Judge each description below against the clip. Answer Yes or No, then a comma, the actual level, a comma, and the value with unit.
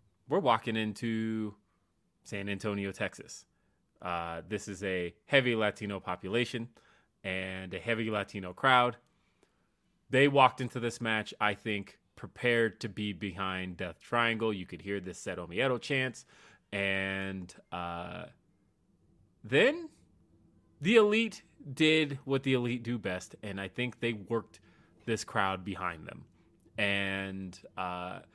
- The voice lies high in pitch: No, low, 105 Hz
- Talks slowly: Yes, slow, 125 wpm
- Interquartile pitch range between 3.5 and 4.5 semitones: Yes, average, 4.0 semitones